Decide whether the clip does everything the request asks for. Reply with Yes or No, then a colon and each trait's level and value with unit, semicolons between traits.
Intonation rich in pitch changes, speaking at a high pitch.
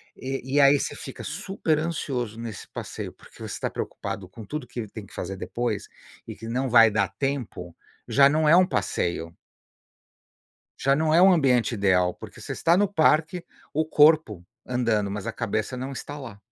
No: wide, 6.1 semitones; low, 125 Hz